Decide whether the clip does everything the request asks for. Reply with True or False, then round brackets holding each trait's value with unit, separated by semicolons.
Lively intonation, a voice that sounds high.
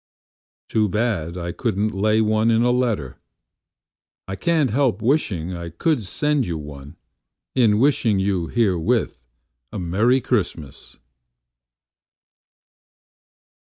False (5.7 semitones; 105 Hz)